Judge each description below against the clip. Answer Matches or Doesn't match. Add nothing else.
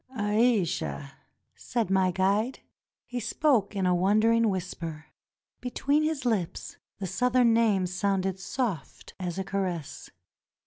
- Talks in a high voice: Matches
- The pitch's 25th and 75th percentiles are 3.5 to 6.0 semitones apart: Matches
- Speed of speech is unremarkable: Doesn't match